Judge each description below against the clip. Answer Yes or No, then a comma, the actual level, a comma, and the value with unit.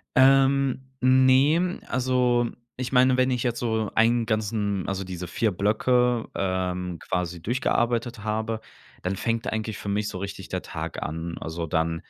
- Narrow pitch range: No, average, 4.9 semitones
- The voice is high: No, low, 110 Hz